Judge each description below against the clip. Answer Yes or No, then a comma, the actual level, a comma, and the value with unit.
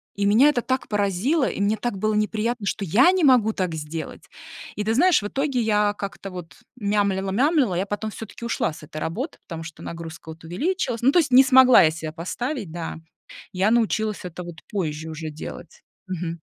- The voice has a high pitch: Yes, high, 205 Hz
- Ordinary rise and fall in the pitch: No, wide, 6.2 semitones